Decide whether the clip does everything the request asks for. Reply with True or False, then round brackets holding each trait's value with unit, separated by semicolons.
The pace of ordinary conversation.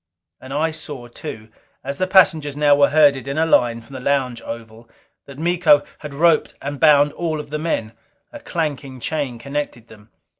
True (185 wpm)